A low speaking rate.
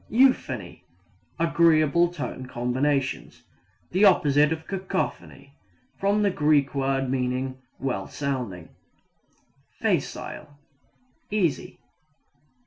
Yes: slow, 80 wpm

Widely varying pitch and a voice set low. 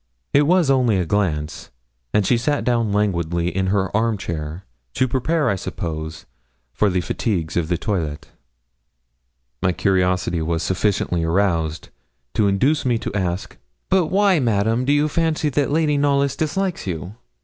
Yes: wide, 8.1 semitones; low, 100 Hz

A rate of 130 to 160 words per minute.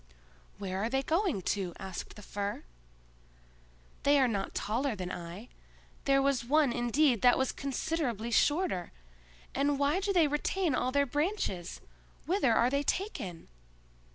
Yes: average, 140 wpm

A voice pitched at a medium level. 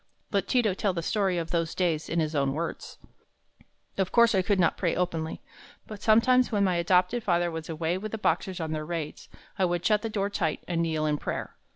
Yes: medium, 180 Hz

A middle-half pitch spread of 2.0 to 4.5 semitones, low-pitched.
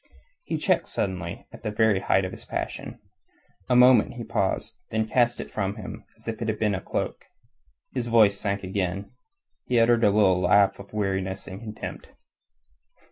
Yes: average, 2.9 semitones; low, 105 Hz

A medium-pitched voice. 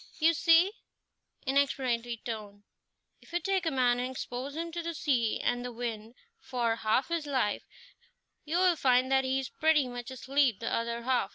No: very high, 260 Hz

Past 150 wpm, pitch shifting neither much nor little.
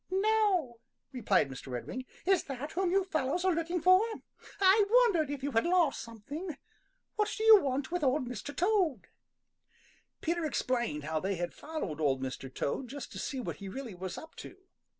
No: average, 180 wpm; wide, 8.2 semitones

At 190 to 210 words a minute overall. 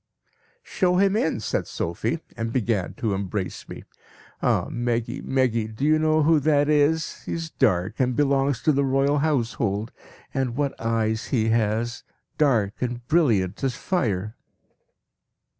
No: average, 145 wpm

